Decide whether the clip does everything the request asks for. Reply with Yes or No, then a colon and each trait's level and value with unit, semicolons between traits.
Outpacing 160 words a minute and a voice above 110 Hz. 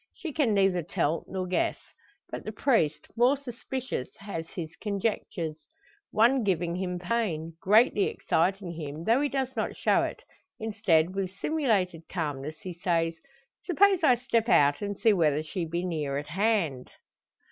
No: average, 155 wpm; medium, 185 Hz